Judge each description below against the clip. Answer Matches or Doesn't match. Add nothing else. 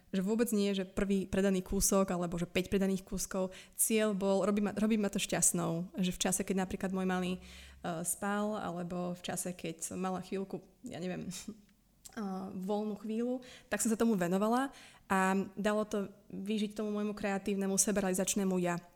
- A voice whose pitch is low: Doesn't match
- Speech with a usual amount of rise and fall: Doesn't match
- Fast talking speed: Matches